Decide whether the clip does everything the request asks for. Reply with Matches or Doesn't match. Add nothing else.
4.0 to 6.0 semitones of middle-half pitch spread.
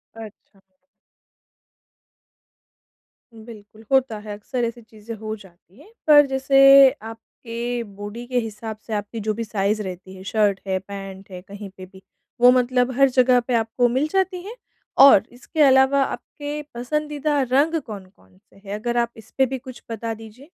Matches